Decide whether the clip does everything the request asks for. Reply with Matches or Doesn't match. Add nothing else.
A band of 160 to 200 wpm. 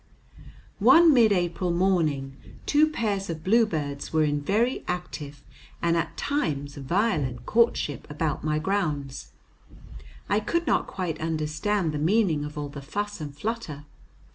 Doesn't match